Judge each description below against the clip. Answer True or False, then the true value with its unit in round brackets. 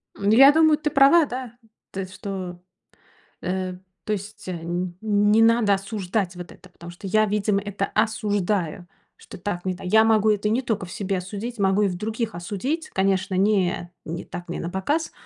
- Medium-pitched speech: False (200 Hz)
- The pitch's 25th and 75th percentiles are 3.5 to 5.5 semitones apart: False (3.0 semitones)